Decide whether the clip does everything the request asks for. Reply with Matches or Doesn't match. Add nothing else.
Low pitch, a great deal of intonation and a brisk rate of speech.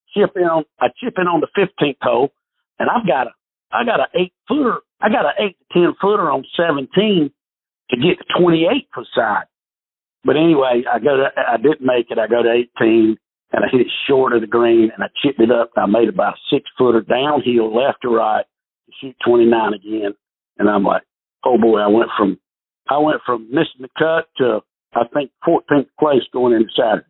Matches